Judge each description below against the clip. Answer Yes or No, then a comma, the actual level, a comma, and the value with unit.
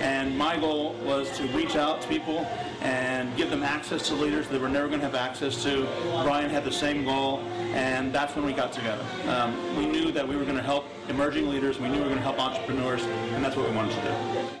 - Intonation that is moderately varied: No, narrow, 1.7 semitones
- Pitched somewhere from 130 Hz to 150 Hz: Yes, low, 135 Hz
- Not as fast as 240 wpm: No, fast, 250 wpm